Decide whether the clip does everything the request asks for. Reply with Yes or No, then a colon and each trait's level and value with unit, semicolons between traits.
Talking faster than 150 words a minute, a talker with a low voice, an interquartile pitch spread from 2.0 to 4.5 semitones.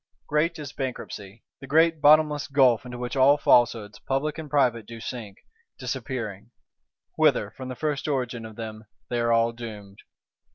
Yes: average, 160 wpm; low, 125 Hz; average, 4.0 semitones